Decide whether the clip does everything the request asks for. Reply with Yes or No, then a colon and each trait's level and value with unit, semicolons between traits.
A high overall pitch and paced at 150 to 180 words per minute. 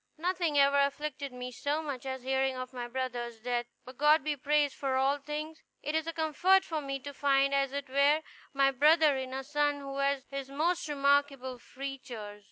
No: very high, 275 Hz; average, 195 wpm